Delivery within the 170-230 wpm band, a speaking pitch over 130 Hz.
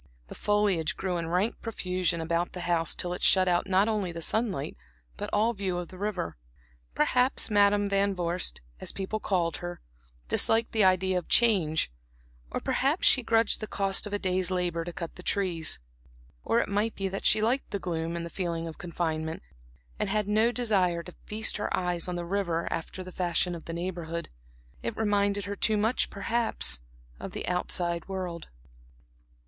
Yes: average, 185 wpm; medium, 185 Hz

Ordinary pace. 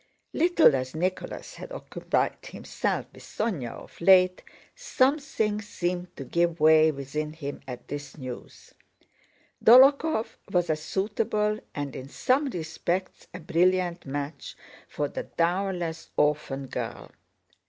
No: slow, 120 wpm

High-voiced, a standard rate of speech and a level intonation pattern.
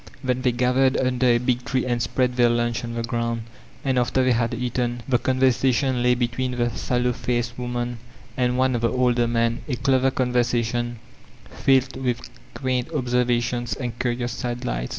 No: low, 125 Hz; average, 180 wpm; narrow, 1.2 semitones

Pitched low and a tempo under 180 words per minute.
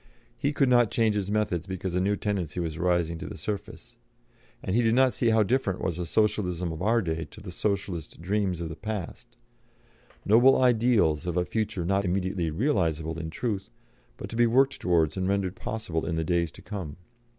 No: very low, 95 Hz; average, 200 wpm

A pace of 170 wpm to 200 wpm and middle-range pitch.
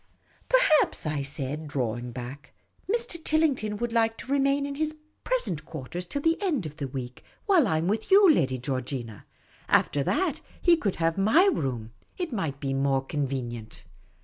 Yes: average, 180 wpm; medium, 160 Hz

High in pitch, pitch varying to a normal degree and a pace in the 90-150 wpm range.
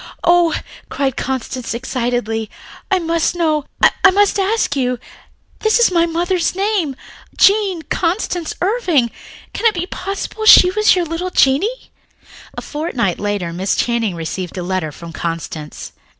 No: very high, 325 Hz; wide, 8.2 semitones; average, 140 wpm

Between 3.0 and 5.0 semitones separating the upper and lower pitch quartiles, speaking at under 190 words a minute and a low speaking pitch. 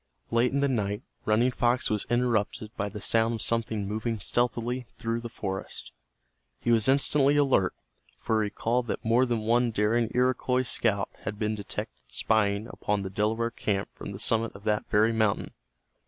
No: narrow, 2.4 semitones; average, 175 wpm; low, 115 Hz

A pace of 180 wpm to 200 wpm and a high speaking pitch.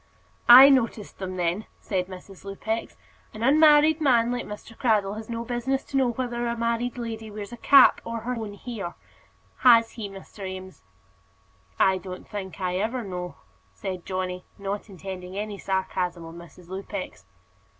No: average, 160 wpm; high, 210 Hz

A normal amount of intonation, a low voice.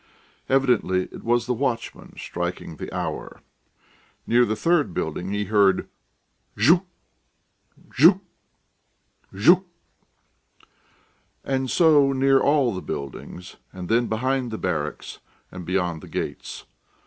No: wide, 6.6 semitones; low, 115 Hz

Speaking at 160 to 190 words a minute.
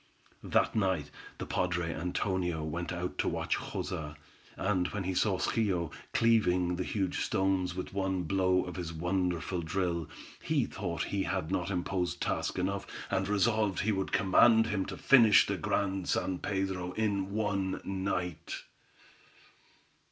No: average, 145 wpm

